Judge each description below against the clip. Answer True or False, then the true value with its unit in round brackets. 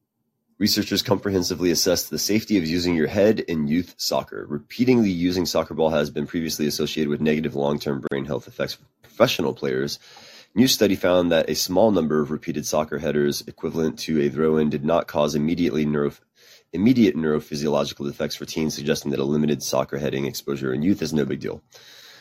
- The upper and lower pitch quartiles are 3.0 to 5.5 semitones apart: False (2.6 semitones)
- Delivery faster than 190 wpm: False (185 wpm)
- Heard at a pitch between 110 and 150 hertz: False (75 Hz)